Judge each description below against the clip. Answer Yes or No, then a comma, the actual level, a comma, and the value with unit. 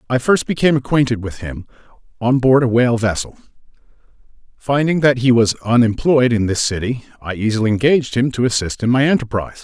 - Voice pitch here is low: Yes, low, 120 Hz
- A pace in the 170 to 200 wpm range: Yes, average, 175 wpm